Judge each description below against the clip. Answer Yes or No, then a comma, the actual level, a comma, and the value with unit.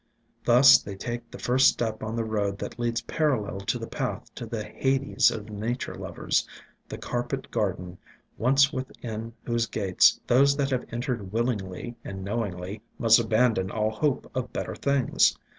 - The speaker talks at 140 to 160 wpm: No, average, 170 wpm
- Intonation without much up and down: No, average, 3.3 semitones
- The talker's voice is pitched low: Yes, low, 115 Hz